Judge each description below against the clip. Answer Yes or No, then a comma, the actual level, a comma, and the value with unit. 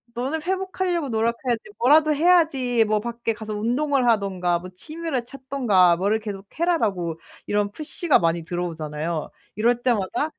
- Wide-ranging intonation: Yes, wide, 7.0 semitones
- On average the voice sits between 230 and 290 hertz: Yes, high, 235 Hz